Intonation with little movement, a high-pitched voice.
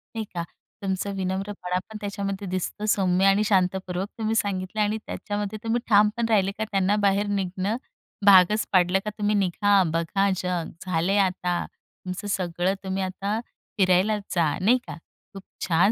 Yes: narrow, 2.0 semitones; high, 195 Hz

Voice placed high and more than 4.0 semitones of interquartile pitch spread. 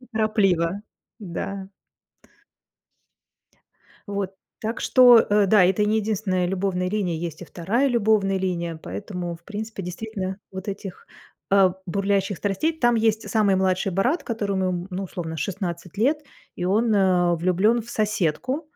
No: high, 195 Hz; average, 3.2 semitones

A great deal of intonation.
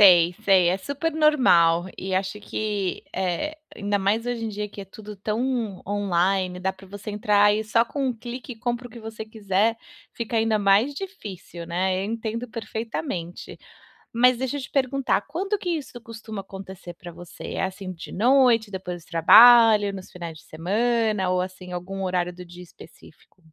No: average, 4.1 semitones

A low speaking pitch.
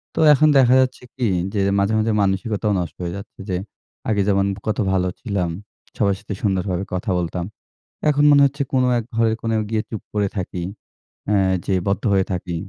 Yes: low, 100 Hz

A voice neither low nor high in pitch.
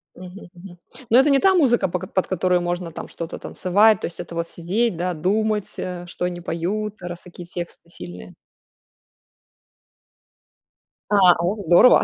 Yes: medium, 180 Hz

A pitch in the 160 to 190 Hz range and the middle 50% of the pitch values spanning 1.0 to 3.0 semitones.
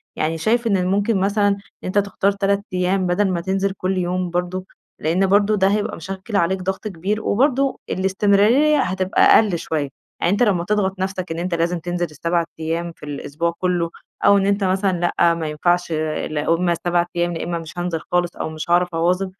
Yes: medium, 185 Hz; narrow, 2.6 semitones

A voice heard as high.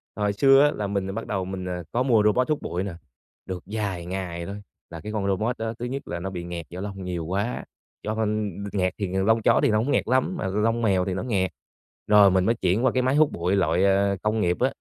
No: low, 100 Hz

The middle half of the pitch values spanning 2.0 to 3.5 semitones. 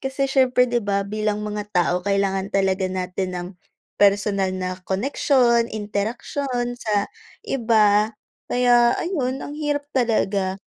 No: average, 4.1 semitones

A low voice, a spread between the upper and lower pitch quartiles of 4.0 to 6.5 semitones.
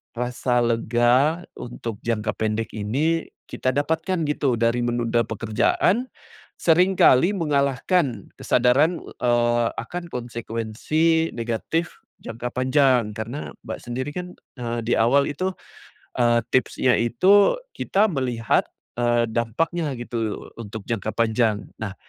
Yes: low, 120 Hz; average, 4.7 semitones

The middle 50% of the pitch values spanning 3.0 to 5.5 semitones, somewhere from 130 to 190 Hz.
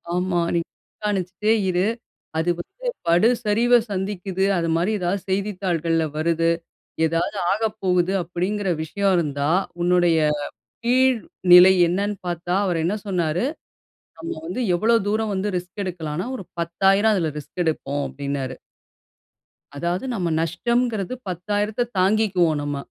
Yes: average, 3.6 semitones; medium, 185 Hz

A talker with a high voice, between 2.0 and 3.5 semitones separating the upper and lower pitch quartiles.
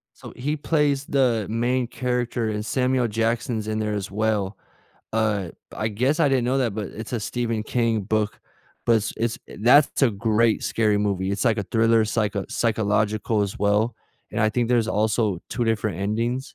No: low, 110 Hz; narrow, 2.4 semitones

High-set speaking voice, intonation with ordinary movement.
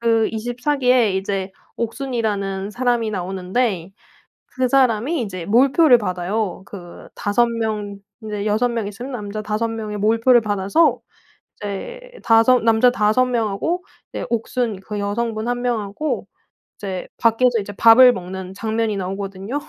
Yes: high, 220 Hz; average, 3.3 semitones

